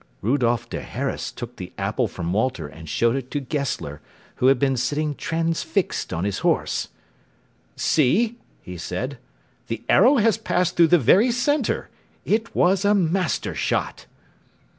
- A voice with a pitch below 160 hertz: Yes, medium, 140 Hz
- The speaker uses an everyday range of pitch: No, wide, 7.9 semitones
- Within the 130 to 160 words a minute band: Yes, average, 150 wpm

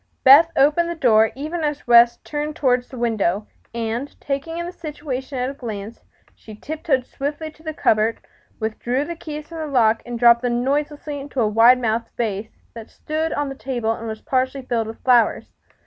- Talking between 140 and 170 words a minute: No, average, 195 wpm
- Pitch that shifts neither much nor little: Yes, average, 4.4 semitones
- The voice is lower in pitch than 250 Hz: No, very high, 255 Hz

